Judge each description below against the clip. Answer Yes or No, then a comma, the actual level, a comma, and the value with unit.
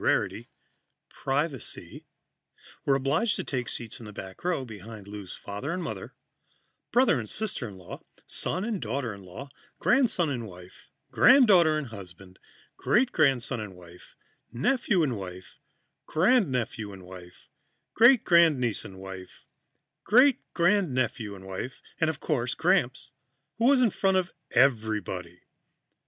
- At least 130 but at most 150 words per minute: Yes, average, 140 wpm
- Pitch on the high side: No, low, 130 Hz